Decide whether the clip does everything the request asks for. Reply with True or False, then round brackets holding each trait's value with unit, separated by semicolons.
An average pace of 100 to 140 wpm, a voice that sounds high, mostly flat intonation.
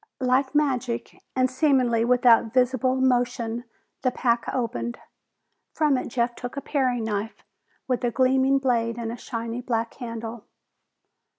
True (135 wpm; 245 Hz; 1.9 semitones)